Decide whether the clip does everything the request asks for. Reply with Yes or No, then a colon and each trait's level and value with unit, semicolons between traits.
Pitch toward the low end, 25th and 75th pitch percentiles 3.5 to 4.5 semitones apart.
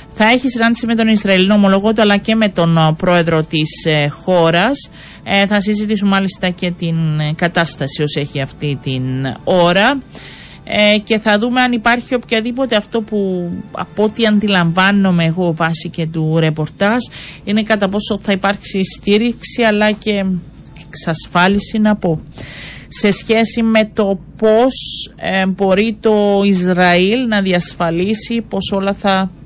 No: high, 195 Hz; average, 4.2 semitones